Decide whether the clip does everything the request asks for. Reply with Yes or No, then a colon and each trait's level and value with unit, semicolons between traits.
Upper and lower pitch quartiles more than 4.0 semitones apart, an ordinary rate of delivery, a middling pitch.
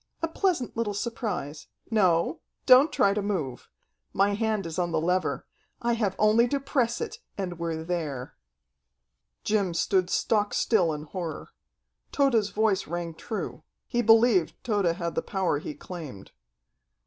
No: average, 5.1 semitones; average, 150 wpm; high, 195 Hz